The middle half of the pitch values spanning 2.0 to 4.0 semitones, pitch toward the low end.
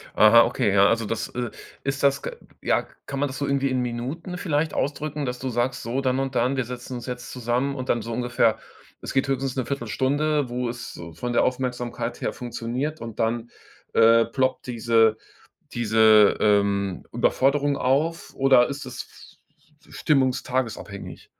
Yes: average, 2.8 semitones; low, 125 Hz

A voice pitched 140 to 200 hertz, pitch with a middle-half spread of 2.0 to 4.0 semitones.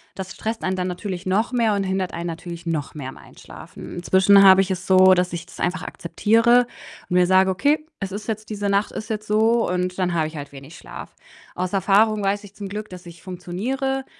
Yes: high, 190 Hz; average, 2.9 semitones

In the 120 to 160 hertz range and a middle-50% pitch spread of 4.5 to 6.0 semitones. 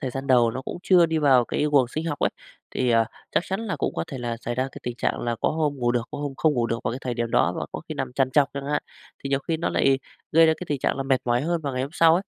No: low, 135 Hz; average, 4.0 semitones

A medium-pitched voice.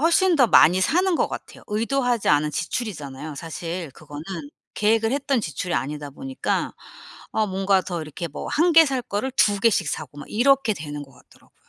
No: high, 200 Hz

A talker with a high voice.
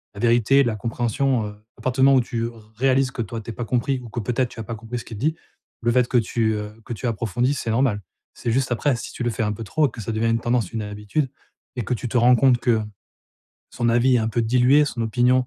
No: low, 120 Hz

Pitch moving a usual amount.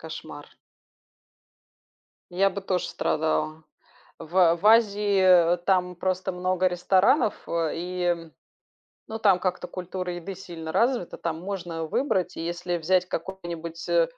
No: narrow, 2.2 semitones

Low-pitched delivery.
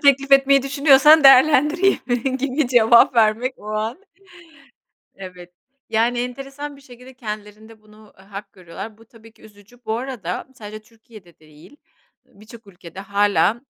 No: high, 230 Hz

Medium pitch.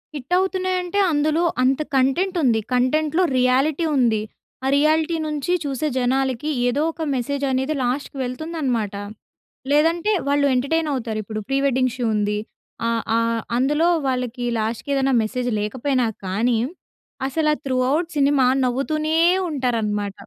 No: very high, 265 Hz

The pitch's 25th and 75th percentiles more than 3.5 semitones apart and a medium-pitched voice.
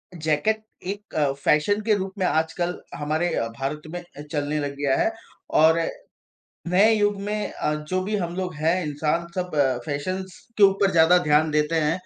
Yes: average, 4.0 semitones; medium, 170 Hz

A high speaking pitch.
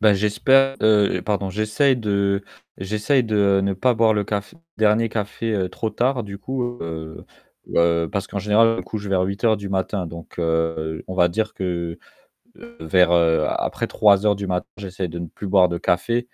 No: low, 100 Hz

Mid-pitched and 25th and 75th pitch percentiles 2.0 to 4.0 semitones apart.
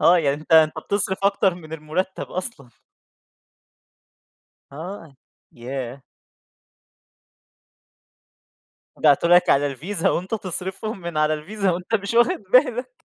No: medium, 175 Hz; average, 4.6 semitones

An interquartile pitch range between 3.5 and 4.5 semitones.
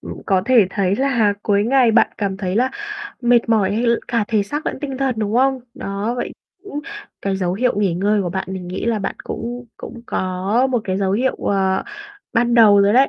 Yes: average, 3.9 semitones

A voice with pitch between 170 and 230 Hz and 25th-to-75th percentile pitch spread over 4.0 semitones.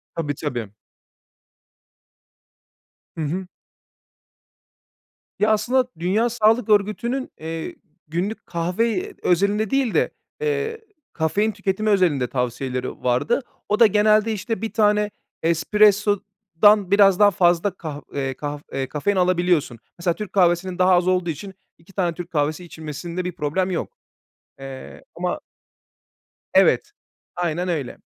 Yes: medium, 185 Hz; average, 4.5 semitones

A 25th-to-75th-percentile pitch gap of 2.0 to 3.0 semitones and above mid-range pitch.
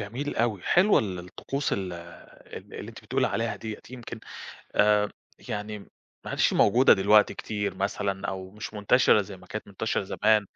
No: narrow, 2.4 semitones; low, 105 Hz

